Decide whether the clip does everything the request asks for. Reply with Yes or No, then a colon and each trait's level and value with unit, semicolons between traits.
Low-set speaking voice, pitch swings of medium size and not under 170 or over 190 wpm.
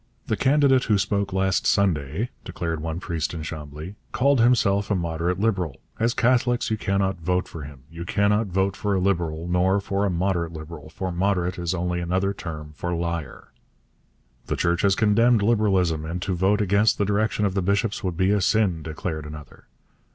Yes: very low, 95 Hz; average, 3.3 semitones; average, 180 wpm